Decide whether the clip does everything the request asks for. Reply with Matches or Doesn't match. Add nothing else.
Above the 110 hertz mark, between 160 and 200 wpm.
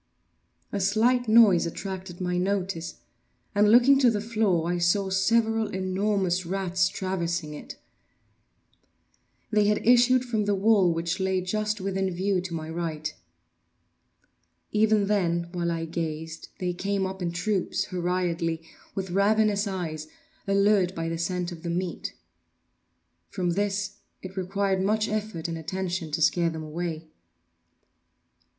Doesn't match